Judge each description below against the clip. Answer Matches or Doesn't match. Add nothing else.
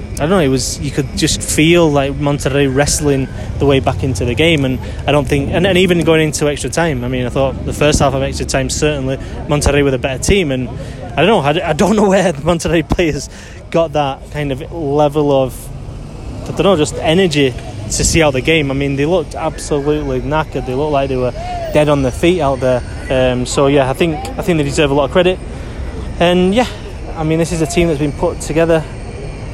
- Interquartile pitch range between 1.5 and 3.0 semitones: Doesn't match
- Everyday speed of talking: Doesn't match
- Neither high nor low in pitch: Matches